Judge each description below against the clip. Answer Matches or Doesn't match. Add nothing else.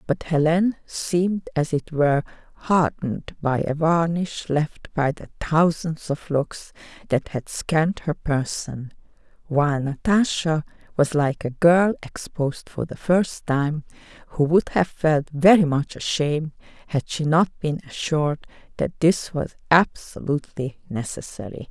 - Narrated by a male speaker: Doesn't match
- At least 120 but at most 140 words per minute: Matches